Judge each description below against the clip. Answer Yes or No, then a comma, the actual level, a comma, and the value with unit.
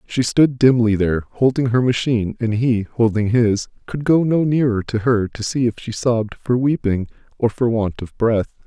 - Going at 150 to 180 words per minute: No, average, 200 wpm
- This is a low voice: Yes, low, 120 Hz